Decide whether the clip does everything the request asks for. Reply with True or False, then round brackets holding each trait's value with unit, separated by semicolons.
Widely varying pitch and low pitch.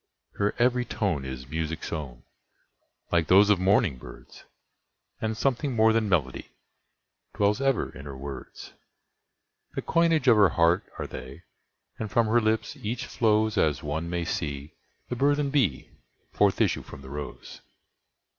True (7.6 semitones; 100 Hz)